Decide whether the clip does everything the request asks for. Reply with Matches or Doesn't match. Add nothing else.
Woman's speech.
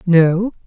Matches